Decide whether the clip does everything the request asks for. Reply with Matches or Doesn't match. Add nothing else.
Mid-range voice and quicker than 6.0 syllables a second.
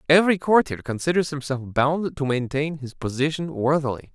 Doesn't match